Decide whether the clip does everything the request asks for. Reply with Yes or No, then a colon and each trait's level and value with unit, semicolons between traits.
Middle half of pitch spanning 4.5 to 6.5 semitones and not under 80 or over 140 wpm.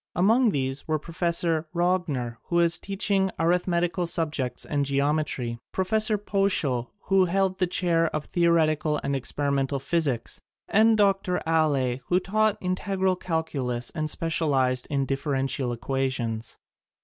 Yes: average, 5.2 semitones; slow, 135 wpm